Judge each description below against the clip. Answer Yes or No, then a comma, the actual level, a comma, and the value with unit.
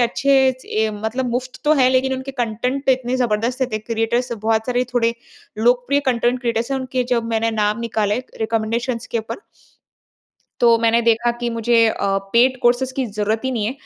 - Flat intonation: Yes, narrow, 2.2 semitones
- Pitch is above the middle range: Yes, high, 235 Hz